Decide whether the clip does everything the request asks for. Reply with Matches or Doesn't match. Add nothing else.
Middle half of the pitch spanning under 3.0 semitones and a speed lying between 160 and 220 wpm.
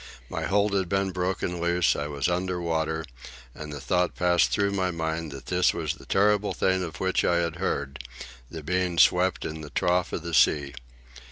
Matches